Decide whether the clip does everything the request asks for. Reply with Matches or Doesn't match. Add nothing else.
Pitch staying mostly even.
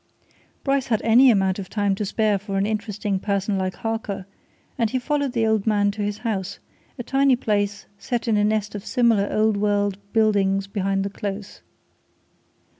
Matches